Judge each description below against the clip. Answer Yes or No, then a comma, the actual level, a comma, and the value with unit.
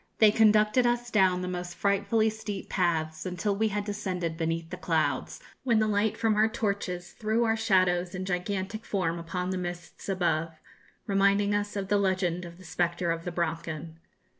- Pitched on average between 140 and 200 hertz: Yes, medium, 185 Hz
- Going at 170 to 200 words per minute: Yes, average, 180 wpm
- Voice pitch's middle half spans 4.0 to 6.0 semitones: No, average, 3.3 semitones